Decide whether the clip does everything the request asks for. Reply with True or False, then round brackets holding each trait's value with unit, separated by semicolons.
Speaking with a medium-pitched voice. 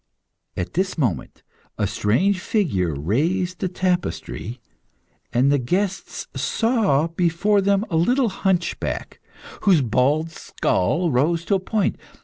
True (170 Hz)